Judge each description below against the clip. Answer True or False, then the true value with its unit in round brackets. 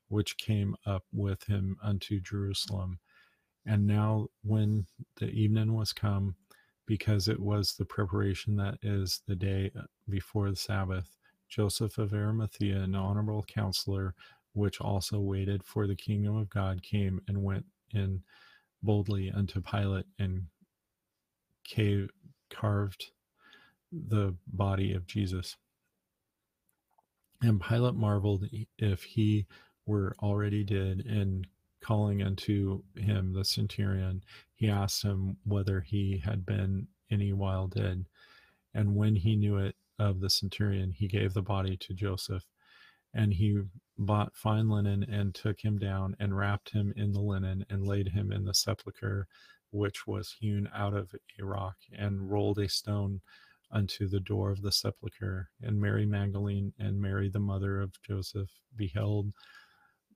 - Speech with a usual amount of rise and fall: False (1.3 semitones)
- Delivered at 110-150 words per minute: True (140 wpm)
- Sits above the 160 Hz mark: False (100 Hz)